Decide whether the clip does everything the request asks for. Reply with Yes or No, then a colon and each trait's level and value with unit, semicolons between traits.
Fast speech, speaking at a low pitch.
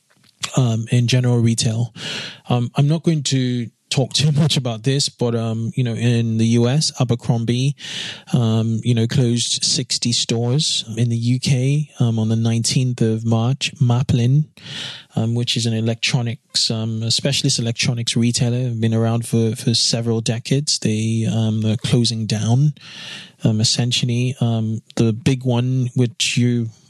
No: average, 150 wpm; low, 120 Hz